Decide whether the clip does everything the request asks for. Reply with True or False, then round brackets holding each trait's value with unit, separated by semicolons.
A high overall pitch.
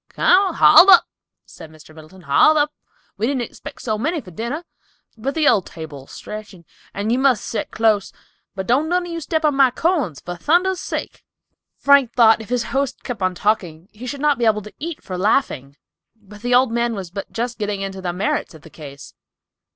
True (225 Hz)